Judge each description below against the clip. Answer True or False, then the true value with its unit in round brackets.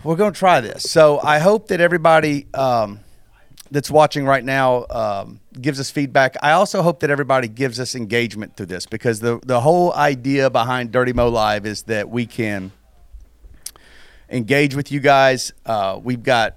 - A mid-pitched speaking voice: False (130 Hz)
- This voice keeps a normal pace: True (180 wpm)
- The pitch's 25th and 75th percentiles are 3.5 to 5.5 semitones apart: True (4.2 semitones)